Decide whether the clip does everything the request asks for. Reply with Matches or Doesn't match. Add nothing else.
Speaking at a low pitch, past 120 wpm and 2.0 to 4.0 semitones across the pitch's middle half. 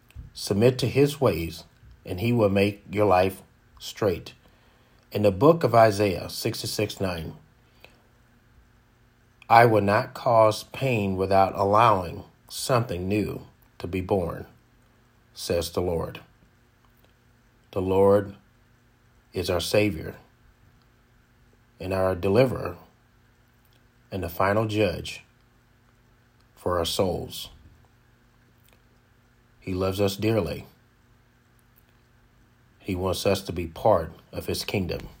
Doesn't match